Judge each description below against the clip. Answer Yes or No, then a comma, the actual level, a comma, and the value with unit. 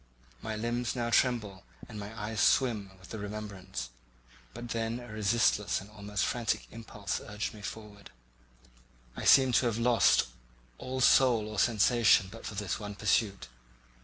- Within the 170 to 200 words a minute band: No, average, 155 wpm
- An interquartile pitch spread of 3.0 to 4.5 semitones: No, narrow, 2.4 semitones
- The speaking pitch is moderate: No, low, 110 Hz